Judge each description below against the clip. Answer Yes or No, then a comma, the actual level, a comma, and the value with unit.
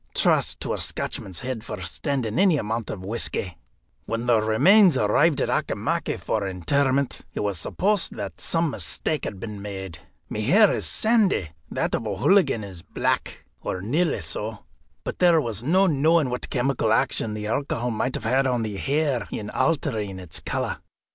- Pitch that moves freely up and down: Yes, wide, 6.2 semitones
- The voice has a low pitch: Yes, low, 115 Hz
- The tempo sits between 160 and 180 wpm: Yes, average, 165 wpm